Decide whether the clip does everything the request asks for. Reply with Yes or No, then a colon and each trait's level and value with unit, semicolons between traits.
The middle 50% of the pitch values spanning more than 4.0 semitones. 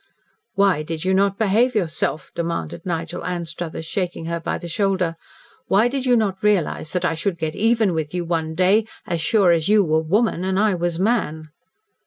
No: average, 3.5 semitones